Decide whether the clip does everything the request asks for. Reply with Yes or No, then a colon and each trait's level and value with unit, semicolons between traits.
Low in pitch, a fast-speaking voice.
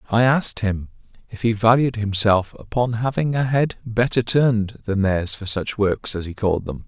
No: low, 110 Hz; average, 190 wpm